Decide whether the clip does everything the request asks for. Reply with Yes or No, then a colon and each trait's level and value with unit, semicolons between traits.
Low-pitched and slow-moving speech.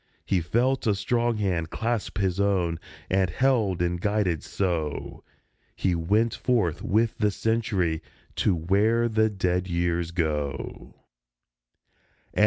Yes: very low, 95 Hz; slow, 130 wpm